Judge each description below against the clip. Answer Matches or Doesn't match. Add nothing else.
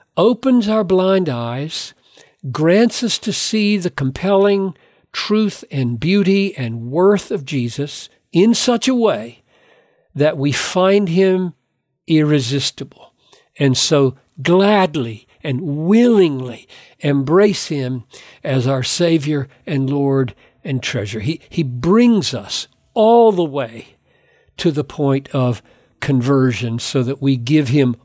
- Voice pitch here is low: Doesn't match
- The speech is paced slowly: Matches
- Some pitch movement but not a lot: Doesn't match